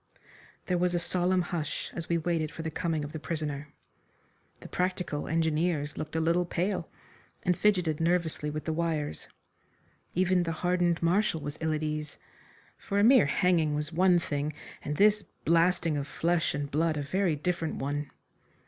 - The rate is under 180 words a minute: Yes, average, 170 wpm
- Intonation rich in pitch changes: No, average, 2.7 semitones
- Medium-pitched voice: Yes, medium, 165 Hz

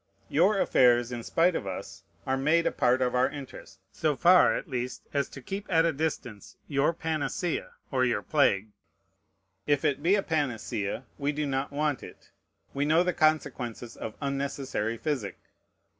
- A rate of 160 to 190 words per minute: Yes, average, 170 wpm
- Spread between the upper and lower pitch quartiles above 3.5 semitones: Yes, average, 4.1 semitones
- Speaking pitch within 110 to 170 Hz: Yes, medium, 140 Hz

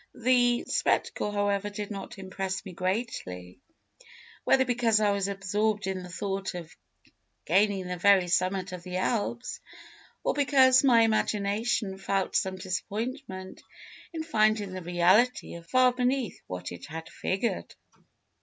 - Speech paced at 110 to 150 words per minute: Yes, slow, 135 wpm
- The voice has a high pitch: Yes, high, 200 Hz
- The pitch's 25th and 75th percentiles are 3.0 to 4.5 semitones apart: Yes, average, 3.8 semitones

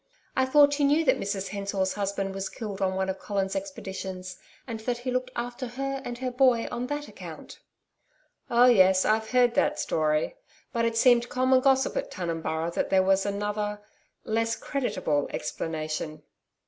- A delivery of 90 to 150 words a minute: No, average, 170 wpm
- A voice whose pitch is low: No, high, 220 Hz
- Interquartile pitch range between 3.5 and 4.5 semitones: No, average, 4.9 semitones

